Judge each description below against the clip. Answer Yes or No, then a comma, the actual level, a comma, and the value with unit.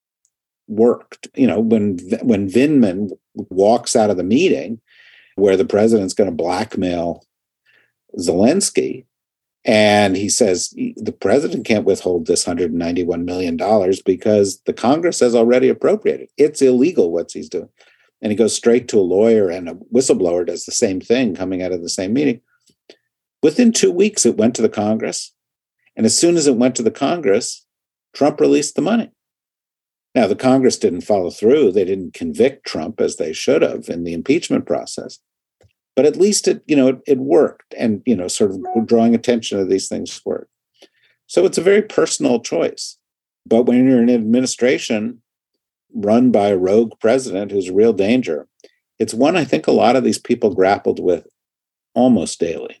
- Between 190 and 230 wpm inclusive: No, average, 175 wpm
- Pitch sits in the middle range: No, low, 125 Hz